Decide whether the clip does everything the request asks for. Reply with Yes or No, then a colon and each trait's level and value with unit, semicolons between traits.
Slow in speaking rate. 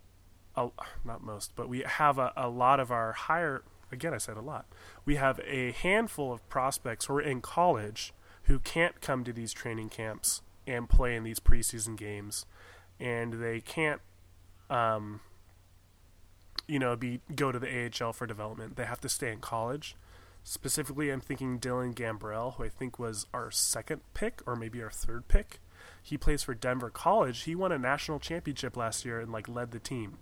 No: average, 185 wpm